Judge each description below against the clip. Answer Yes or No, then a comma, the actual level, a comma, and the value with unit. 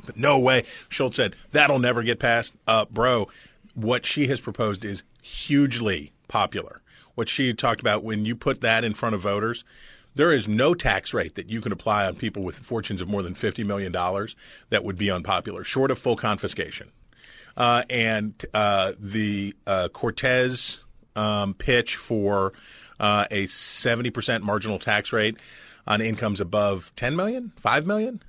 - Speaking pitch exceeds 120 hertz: No, low, 110 Hz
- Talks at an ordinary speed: Yes, average, 165 wpm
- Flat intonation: No, average, 3.2 semitones